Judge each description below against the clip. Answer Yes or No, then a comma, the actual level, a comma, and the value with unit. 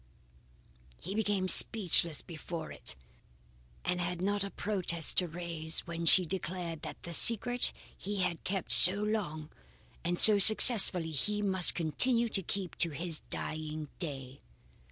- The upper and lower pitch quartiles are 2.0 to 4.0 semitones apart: Yes, average, 3.6 semitones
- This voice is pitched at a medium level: Yes, medium, 180 Hz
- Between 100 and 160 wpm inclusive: Yes, average, 140 wpm